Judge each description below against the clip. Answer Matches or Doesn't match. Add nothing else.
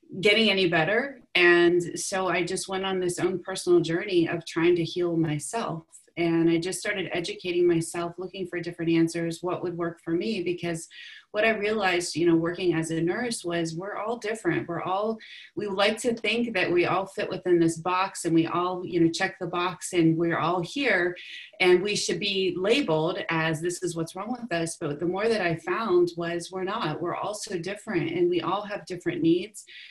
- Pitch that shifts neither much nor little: Doesn't match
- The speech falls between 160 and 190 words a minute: Doesn't match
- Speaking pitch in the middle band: Matches